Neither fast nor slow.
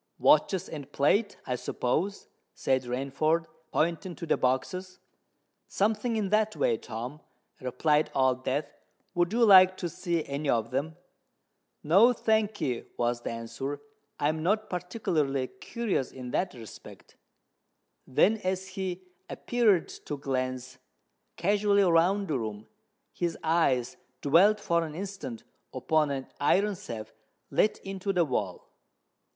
No: slow, 130 wpm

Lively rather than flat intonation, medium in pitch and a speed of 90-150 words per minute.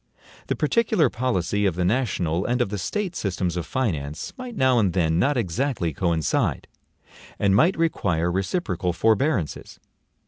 No: wide, 7.2 semitones; low, 100 Hz; average, 145 wpm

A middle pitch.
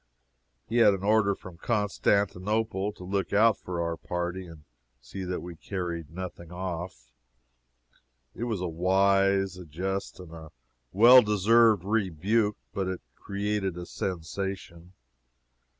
No: very low, 95 Hz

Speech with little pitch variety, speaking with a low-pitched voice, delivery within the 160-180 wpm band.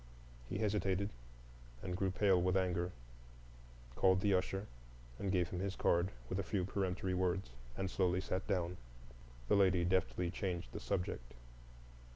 No: narrow, 1.3 semitones; very low, 95 Hz; average, 150 wpm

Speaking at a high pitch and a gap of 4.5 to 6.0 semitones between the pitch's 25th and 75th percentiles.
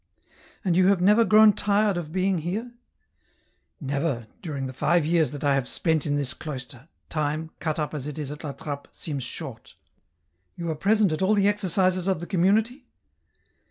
No: medium, 165 Hz; average, 5.1 semitones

